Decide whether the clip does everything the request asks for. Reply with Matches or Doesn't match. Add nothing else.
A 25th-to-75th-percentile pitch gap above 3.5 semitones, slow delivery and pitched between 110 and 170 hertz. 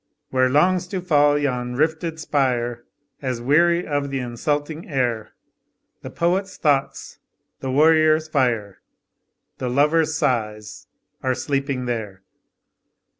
Matches